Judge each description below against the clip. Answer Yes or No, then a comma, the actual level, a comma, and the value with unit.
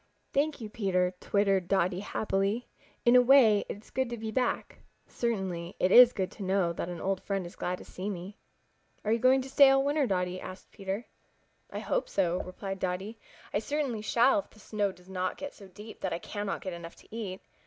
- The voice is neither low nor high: No, high, 200 Hz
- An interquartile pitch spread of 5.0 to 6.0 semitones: No, average, 4.3 semitones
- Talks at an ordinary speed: No, fast, 215 wpm